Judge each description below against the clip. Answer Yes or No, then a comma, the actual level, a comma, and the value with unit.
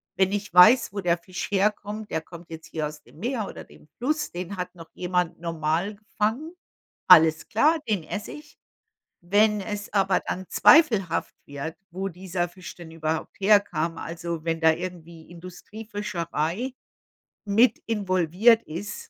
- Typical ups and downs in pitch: Yes, average, 3.9 semitones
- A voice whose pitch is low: No, medium, 185 Hz